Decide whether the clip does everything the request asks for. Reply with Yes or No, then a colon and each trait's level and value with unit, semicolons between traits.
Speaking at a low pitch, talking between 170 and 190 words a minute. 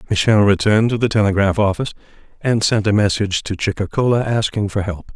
Yes: low, 105 Hz; average, 175 wpm